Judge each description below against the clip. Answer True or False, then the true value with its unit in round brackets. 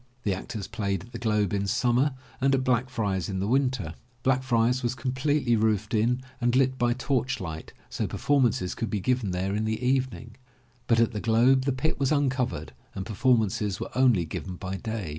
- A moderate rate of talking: True (190 wpm)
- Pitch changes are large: False (4.2 semitones)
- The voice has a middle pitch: False (115 Hz)